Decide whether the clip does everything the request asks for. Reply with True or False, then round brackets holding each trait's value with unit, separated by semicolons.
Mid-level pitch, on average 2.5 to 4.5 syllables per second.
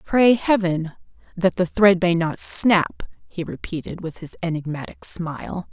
True (180 Hz; 4.2 syllables/s)